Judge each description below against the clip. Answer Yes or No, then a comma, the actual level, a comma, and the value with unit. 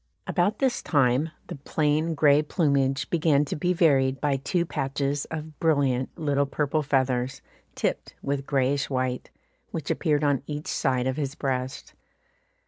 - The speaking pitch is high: No, medium, 140 Hz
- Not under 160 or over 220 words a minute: No, average, 145 wpm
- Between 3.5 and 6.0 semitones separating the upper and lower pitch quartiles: No, narrow, 2.4 semitones